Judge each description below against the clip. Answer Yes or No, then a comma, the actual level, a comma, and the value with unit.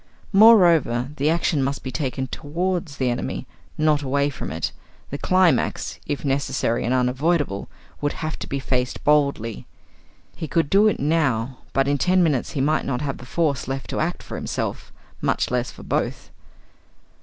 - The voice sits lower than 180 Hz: Yes, medium, 140 Hz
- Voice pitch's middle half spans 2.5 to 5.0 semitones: Yes, average, 3.7 semitones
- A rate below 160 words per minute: No, average, 170 wpm